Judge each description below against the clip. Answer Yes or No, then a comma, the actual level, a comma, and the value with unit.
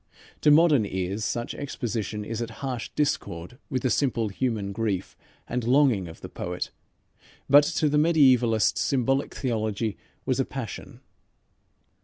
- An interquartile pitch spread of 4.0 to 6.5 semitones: Yes, average, 4.6 semitones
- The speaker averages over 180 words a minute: No, average, 140 wpm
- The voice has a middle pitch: No, low, 120 Hz